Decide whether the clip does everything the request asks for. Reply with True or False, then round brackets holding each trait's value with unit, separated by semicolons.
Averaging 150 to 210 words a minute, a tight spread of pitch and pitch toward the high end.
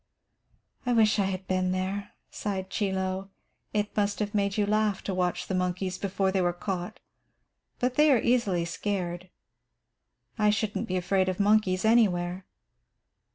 True (155 wpm; 2.2 semitones; 195 Hz)